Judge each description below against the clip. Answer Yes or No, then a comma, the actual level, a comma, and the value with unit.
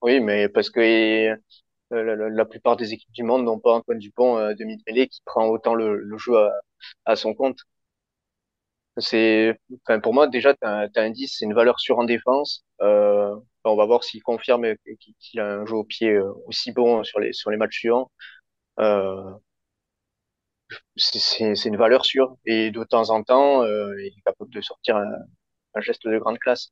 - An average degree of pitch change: No, narrow, 2.1 semitones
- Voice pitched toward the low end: Yes, low, 110 Hz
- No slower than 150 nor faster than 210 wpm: Yes, average, 190 wpm